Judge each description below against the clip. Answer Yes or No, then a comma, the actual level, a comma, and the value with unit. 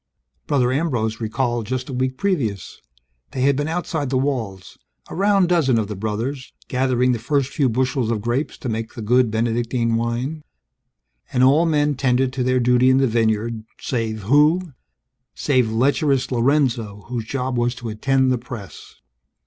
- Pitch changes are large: No, average, 3.1 semitones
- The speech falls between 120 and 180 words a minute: Yes, average, 170 wpm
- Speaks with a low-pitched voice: Yes, low, 125 Hz